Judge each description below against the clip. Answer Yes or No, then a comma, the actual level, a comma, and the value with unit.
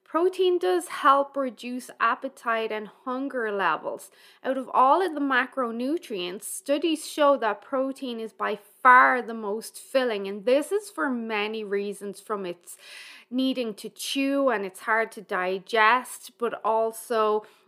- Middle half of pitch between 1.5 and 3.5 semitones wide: No, average, 4.3 semitones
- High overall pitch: Yes, very high, 250 Hz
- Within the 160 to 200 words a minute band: No, average, 145 wpm